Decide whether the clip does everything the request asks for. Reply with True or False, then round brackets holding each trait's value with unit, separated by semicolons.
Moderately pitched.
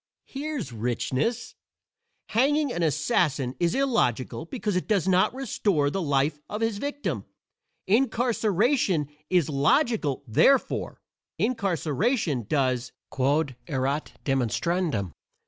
True (170 Hz)